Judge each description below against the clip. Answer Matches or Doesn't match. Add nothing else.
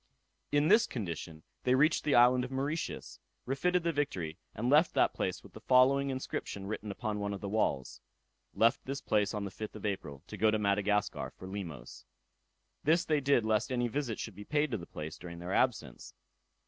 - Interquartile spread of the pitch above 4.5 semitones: Matches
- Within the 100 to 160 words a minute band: Doesn't match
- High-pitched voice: Doesn't match